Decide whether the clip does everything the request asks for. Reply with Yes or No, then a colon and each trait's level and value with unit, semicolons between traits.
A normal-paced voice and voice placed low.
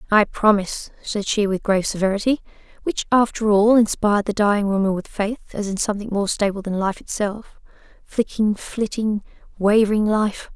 No: average, 155 wpm; high, 210 Hz